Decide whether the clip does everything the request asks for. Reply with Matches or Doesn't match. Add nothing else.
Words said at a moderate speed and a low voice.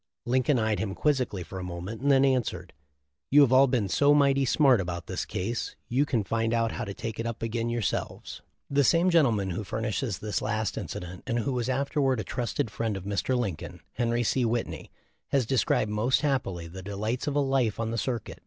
Doesn't match